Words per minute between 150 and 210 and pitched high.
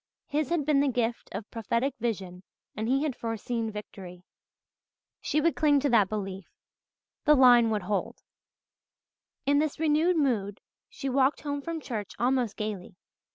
Yes: average, 155 wpm; high, 245 Hz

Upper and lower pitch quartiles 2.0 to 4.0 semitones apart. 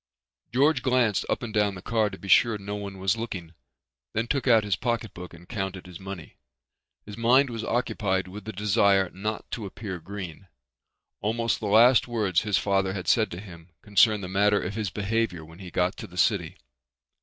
Yes: average, 3.1 semitones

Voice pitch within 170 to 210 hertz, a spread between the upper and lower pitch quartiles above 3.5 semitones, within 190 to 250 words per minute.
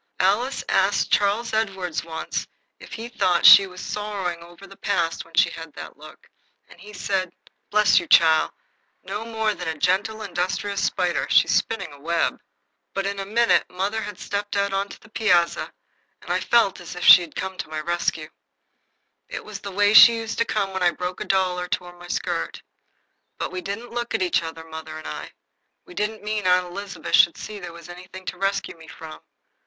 No: high, 190 Hz; average, 3.1 semitones; average, 200 wpm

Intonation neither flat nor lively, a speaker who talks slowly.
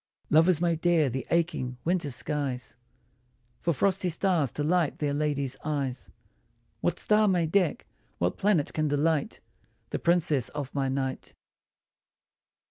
Yes: average, 3.8 semitones; slow, 130 wpm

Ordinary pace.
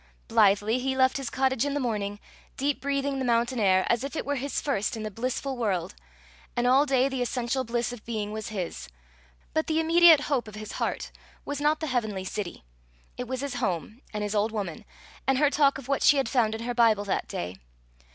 No: fast, 220 wpm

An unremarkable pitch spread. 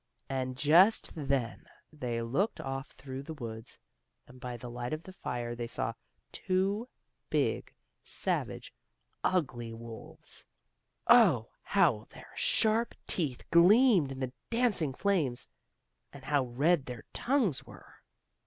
No: wide, 7.2 semitones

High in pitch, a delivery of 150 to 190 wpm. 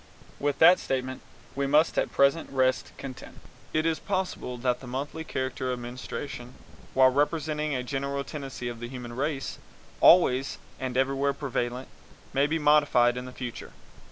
No: low, 135 Hz; average, 155 wpm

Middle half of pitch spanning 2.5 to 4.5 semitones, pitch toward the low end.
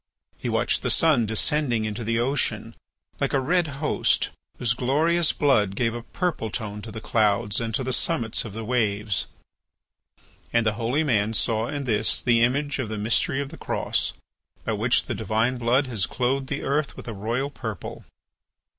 Yes: average, 3.8 semitones; low, 120 Hz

